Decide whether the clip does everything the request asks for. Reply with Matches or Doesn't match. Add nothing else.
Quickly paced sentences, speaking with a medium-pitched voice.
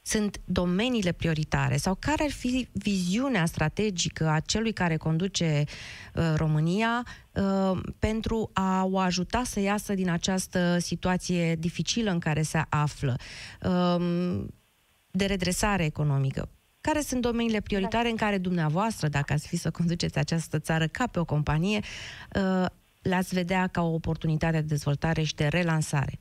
Doesn't match